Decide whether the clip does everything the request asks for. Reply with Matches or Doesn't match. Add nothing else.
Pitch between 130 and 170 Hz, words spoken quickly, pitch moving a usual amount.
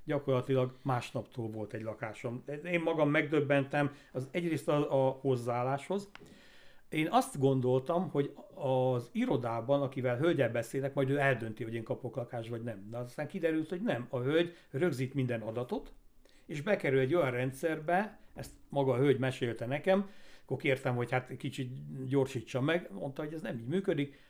Matches